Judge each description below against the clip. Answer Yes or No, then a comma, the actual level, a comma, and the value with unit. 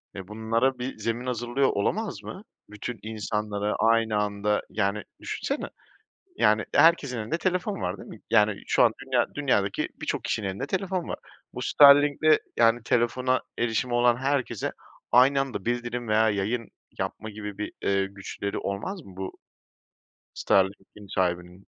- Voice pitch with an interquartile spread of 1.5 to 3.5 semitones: No, average, 3.9 semitones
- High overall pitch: No, low, 115 Hz